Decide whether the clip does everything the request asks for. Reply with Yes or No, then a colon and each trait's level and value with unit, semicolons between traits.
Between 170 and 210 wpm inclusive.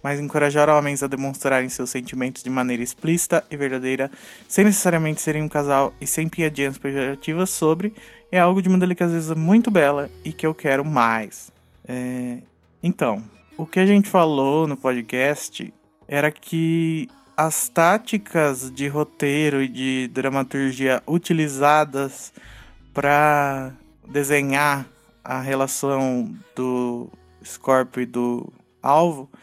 No: average, 125 wpm